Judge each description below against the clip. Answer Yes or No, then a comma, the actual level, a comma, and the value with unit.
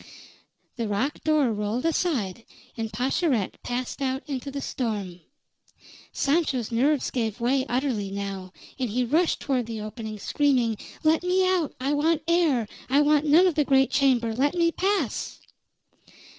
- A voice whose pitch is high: Yes, very high, 265 Hz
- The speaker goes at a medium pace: Yes, average, 150 wpm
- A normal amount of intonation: Yes, average, 4.9 semitones